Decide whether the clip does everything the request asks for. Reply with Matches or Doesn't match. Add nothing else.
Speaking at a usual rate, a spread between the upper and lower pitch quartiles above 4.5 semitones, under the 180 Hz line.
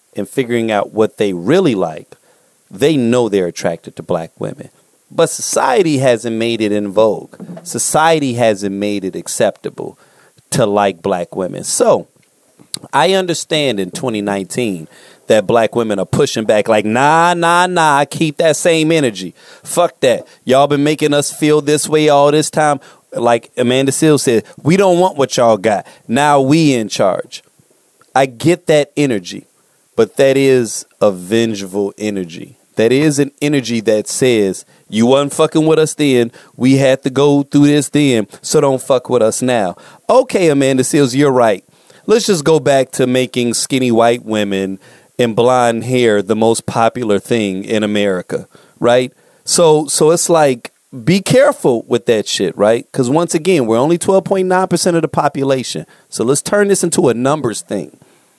Matches